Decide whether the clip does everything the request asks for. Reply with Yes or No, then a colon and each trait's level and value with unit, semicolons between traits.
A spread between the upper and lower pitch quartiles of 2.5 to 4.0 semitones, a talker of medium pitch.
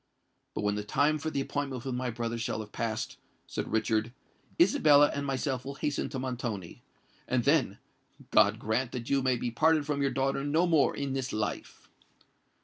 No: average, 3.7 semitones; low, 130 Hz